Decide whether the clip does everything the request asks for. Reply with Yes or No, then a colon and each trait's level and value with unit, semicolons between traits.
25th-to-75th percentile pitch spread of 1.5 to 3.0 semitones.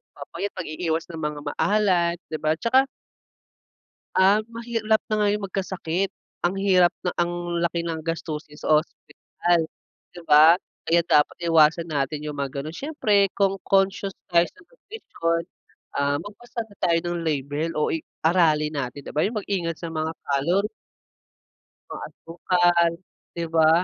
No: average, 3.8 semitones